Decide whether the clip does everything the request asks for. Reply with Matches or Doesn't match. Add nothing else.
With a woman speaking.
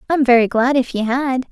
Matches